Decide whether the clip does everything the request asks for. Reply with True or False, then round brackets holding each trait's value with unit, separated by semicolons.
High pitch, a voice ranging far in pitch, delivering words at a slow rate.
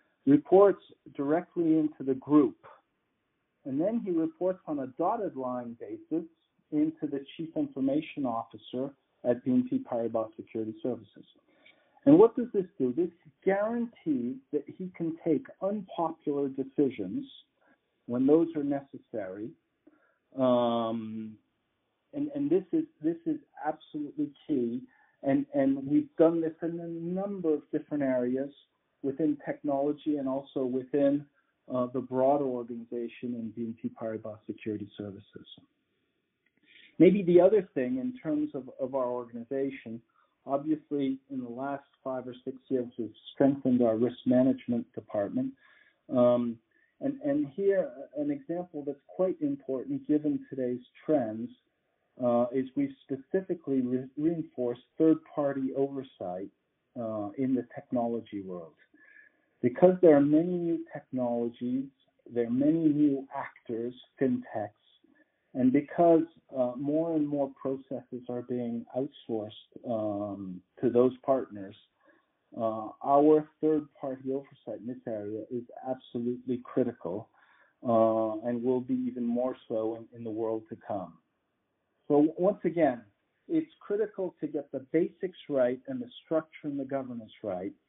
False (140 Hz; 6.4 semitones; 130 wpm)